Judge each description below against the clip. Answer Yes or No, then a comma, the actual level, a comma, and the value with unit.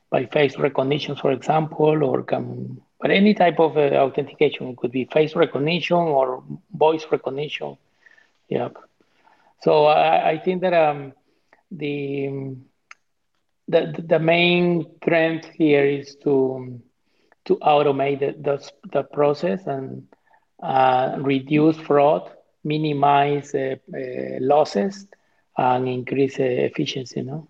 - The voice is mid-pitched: Yes, medium, 145 Hz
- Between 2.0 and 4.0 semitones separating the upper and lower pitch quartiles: Yes, average, 2.9 semitones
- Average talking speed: No, slow, 125 wpm